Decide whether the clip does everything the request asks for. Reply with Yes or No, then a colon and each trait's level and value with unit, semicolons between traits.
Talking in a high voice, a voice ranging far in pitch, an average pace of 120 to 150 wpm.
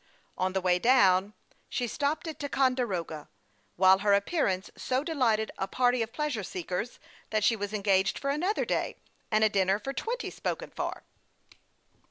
No: high, 215 Hz; wide, 5.7 semitones; average, 165 wpm